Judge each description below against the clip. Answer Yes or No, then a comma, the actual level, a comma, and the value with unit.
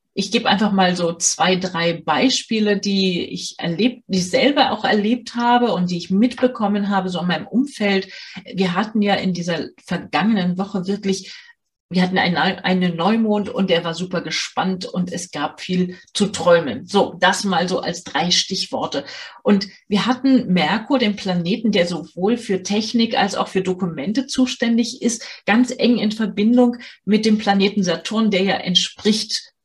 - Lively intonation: No, average, 3.8 semitones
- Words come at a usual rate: Yes, average, 170 wpm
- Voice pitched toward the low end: No, high, 195 Hz